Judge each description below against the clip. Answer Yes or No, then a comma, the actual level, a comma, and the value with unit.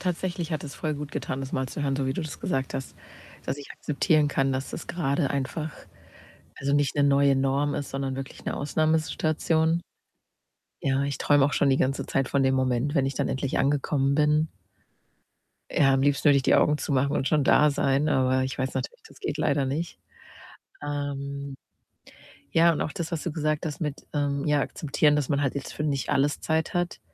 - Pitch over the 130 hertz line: Yes, medium, 140 Hz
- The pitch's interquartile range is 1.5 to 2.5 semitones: Yes, narrow, 2.0 semitones